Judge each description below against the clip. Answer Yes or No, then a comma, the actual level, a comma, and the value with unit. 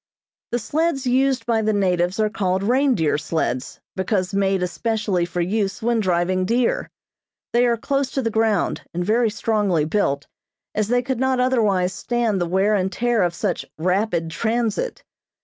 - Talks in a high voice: Yes, high, 210 Hz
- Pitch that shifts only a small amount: No, average, 4.6 semitones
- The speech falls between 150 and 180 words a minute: Yes, average, 165 wpm